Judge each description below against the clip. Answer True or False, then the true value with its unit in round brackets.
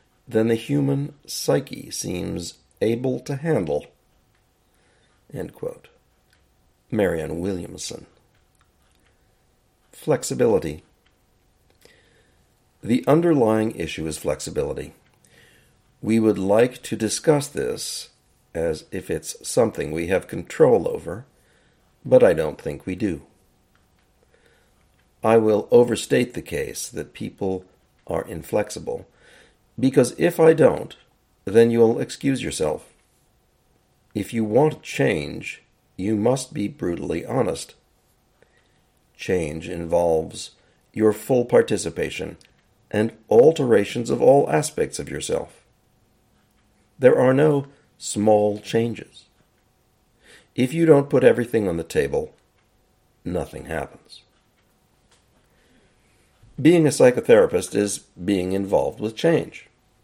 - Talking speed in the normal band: False (95 wpm)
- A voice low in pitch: True (120 Hz)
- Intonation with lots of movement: True (7.3 semitones)